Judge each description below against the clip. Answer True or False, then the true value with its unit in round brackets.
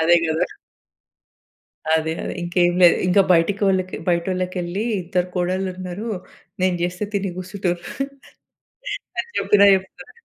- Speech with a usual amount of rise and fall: False (1.6 semitones)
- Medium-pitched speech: True (180 Hz)